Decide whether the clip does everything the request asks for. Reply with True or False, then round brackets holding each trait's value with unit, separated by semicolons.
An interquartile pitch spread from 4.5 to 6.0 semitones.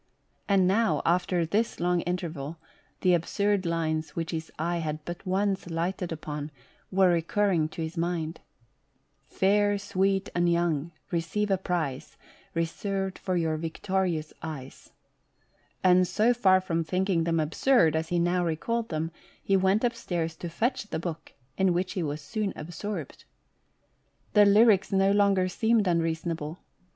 False (3.1 semitones)